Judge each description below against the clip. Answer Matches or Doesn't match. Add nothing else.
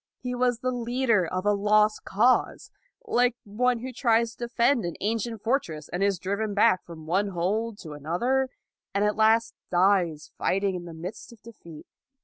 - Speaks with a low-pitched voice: Doesn't match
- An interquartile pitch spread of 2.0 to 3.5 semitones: Doesn't match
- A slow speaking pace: Doesn't match